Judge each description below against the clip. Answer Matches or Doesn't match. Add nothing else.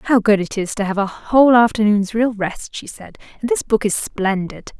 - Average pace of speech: Doesn't match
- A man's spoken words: Doesn't match